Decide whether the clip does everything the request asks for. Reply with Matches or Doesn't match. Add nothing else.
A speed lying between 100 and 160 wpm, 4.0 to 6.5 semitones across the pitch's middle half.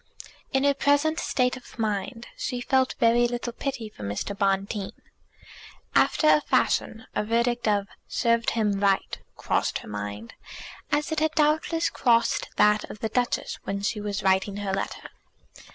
Matches